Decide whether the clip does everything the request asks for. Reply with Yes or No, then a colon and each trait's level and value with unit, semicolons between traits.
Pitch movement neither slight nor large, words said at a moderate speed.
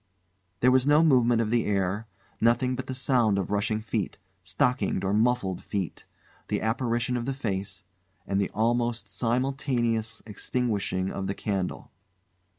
Yes: average, 3.8 semitones; average, 150 wpm